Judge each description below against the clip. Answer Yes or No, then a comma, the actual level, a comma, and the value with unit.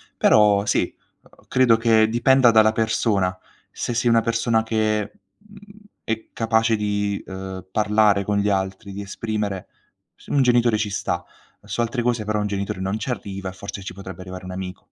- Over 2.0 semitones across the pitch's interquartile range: Yes, narrow, 2.6 semitones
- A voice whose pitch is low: Yes, low, 105 Hz